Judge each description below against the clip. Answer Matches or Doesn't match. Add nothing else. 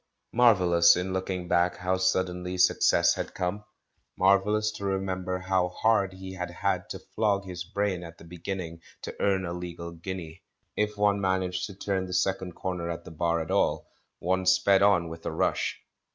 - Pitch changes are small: Matches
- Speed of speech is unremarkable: Matches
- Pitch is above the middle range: Doesn't match